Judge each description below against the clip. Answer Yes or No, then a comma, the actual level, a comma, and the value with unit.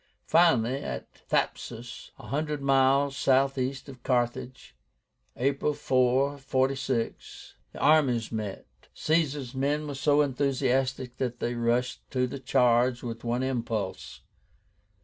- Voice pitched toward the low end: Yes, low, 130 Hz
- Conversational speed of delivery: No, slow, 115 wpm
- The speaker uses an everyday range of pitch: No, narrow, 2.2 semitones